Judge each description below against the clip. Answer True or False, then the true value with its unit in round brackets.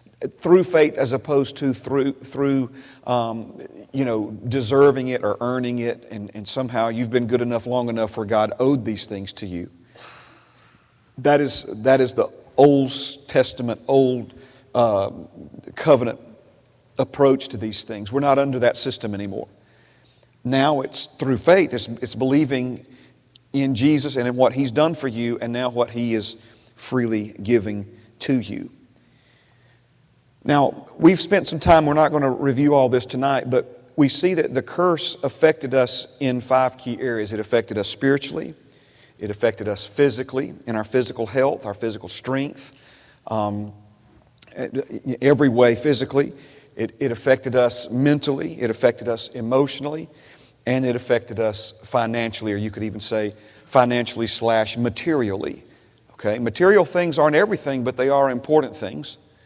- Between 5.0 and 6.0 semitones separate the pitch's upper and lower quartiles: False (3.3 semitones)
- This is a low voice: True (125 Hz)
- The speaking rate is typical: True (155 wpm)